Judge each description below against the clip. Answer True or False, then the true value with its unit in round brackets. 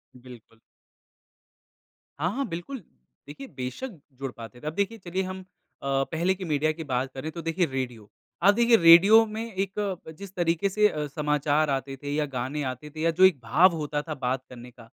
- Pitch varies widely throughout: True (5.8 semitones)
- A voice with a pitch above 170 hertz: False (155 Hz)